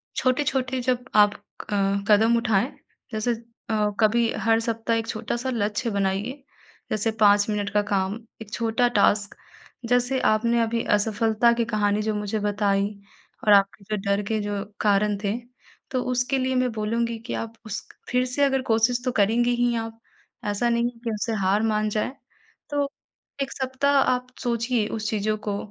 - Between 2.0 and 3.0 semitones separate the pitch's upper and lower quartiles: Yes, average, 2.7 semitones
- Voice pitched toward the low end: No, high, 225 Hz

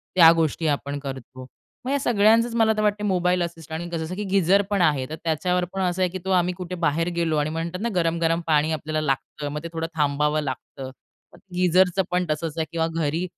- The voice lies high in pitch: No, medium, 165 Hz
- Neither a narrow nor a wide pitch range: Yes, average, 3.1 semitones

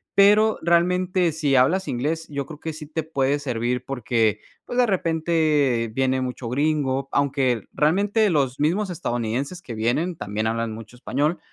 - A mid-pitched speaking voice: Yes, medium, 145 Hz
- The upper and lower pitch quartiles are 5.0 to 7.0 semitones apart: Yes, average, 5.3 semitones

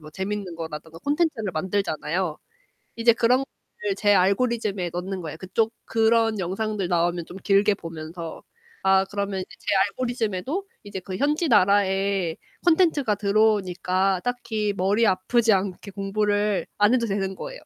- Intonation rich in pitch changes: No, average, 3.3 semitones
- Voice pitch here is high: Yes, high, 200 Hz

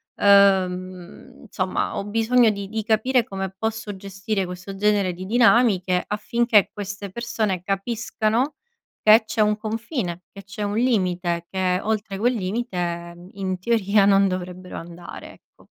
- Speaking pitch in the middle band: No, high, 200 Hz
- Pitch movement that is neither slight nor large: Yes, average, 3.1 semitones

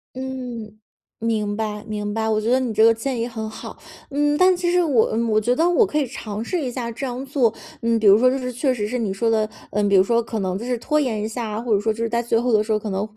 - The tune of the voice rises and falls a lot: No, average, 3.0 semitones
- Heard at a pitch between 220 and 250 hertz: Yes, high, 230 Hz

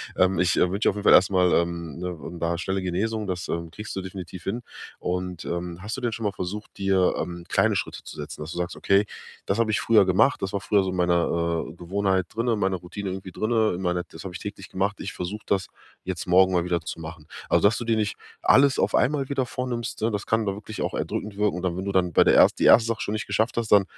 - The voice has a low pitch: Yes, very low, 95 Hz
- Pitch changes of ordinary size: Yes, average, 3.2 semitones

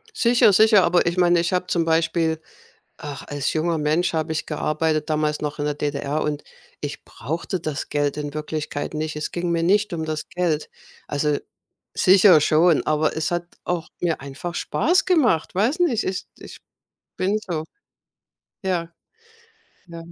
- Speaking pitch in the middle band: Yes, medium, 165 Hz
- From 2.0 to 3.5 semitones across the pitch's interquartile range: Yes, average, 2.8 semitones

